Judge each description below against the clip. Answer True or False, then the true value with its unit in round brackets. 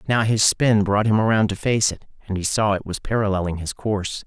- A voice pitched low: True (105 Hz)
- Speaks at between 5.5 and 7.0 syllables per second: True (5.6 syllables/s)